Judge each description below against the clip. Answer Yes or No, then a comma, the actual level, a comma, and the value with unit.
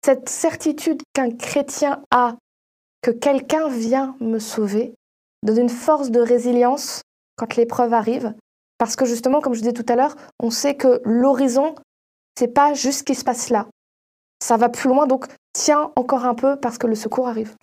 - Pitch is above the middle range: Yes, very high, 255 Hz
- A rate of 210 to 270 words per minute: No, average, 185 wpm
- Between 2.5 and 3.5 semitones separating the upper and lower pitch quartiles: Yes, average, 3.0 semitones